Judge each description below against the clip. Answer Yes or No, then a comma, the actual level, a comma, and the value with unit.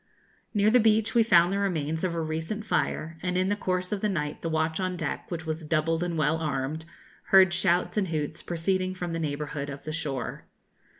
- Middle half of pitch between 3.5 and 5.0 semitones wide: No, average, 3.0 semitones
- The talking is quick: Yes, fast, 215 wpm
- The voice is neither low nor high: Yes, medium, 165 Hz